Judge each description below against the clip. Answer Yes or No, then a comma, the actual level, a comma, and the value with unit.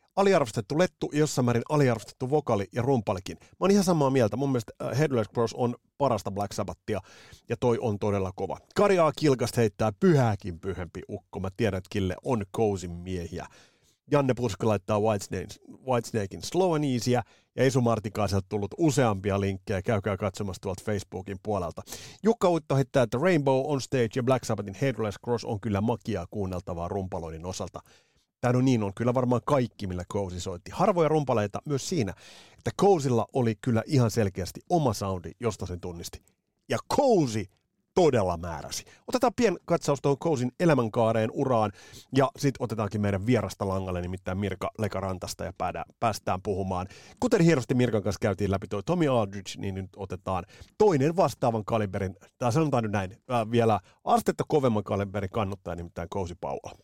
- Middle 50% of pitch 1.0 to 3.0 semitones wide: No, average, 5.2 semitones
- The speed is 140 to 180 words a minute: Yes, fast, 155 wpm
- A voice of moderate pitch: No, low, 110 Hz